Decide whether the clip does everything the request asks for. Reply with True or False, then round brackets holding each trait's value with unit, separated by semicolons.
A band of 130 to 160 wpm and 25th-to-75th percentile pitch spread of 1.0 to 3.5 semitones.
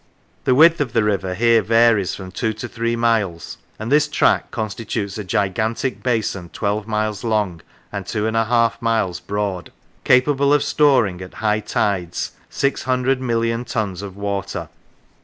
True (155 wpm; 3.0 semitones)